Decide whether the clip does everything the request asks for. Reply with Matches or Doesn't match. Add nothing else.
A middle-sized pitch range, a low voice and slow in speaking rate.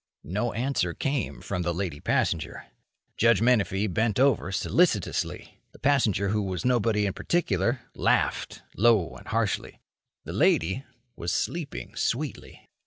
Matches